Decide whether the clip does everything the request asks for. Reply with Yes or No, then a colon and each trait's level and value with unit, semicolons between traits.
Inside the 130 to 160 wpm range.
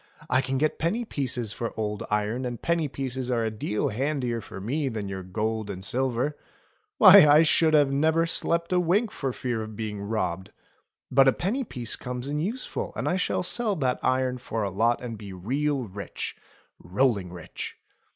No: average, 190 wpm